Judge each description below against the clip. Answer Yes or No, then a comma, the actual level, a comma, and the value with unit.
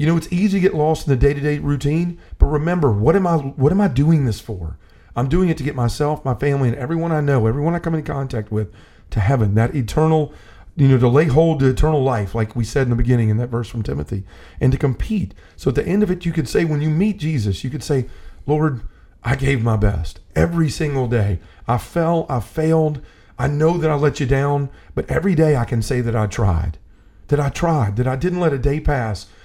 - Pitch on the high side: No, low, 135 Hz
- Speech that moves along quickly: Yes, fast, 245 wpm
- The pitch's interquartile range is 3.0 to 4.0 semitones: No, wide, 5.4 semitones